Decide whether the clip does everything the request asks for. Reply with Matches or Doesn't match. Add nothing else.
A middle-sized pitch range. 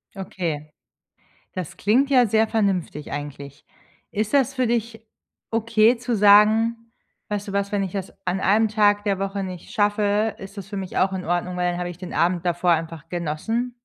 Matches